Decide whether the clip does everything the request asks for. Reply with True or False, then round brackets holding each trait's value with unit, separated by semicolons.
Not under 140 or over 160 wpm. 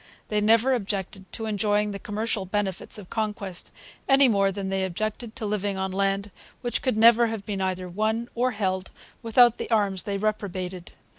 False (175 wpm)